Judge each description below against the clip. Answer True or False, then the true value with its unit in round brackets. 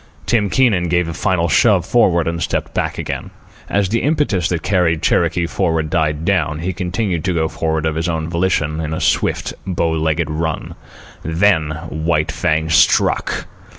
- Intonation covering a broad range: False (2.7 semitones)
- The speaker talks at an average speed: True (170 wpm)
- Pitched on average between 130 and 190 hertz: False (85 Hz)